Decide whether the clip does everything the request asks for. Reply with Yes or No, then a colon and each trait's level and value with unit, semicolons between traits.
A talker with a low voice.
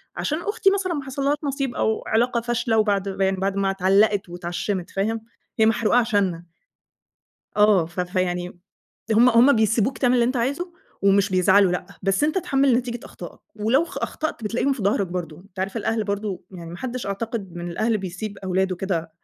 No: high, 210 Hz